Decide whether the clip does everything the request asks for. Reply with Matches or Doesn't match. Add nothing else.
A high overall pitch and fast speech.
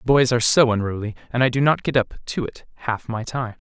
Doesn't match